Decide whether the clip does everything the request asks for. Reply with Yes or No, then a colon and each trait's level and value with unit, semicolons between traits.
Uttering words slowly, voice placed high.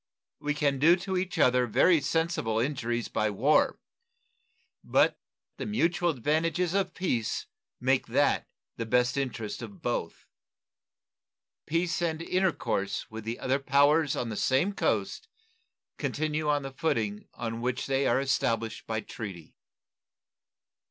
No: slow, 130 wpm; medium, 140 Hz